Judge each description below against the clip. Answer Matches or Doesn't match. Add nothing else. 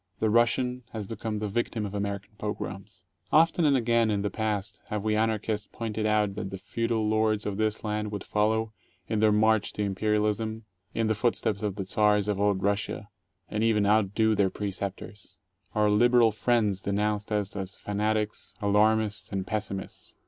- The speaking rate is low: Doesn't match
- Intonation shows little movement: Matches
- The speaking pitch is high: Doesn't match